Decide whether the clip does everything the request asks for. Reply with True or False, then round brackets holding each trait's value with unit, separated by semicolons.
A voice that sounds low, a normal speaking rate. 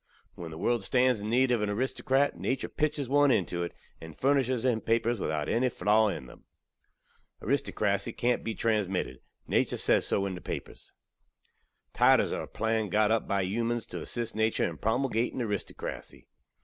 True (110 Hz; 170 wpm)